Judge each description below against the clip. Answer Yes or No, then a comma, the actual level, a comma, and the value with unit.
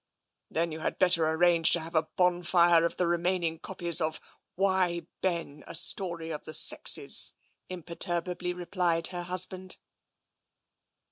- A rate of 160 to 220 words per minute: No, average, 150 wpm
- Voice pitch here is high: No, medium, 175 Hz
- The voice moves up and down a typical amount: No, narrow, 1.5 semitones